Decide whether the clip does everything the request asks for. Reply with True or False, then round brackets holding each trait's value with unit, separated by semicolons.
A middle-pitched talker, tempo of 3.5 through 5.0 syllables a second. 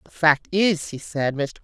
True (160 Hz; 4.4 syllables/s)